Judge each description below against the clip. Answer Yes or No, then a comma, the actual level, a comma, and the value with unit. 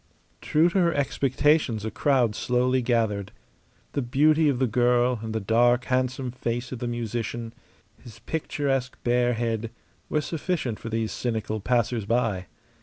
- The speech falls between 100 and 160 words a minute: Yes, average, 150 wpm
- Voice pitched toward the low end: Yes, low, 120 Hz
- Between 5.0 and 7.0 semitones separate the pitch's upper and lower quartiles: No, narrow, 2.5 semitones